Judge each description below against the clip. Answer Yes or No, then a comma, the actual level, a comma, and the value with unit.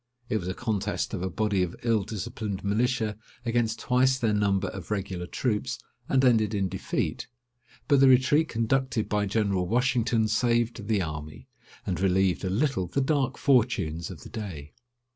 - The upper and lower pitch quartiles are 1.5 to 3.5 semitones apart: No, average, 4.3 semitones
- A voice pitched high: No, low, 110 Hz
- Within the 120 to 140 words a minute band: No, average, 165 wpm